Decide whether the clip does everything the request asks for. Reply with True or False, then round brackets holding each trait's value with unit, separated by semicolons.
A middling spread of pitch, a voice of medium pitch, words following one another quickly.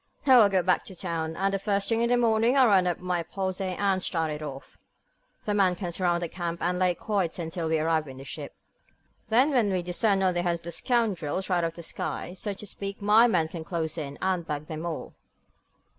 True (3.3 semitones; 180 Hz; 240 wpm)